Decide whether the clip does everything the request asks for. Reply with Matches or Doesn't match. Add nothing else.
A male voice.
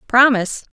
Doesn't match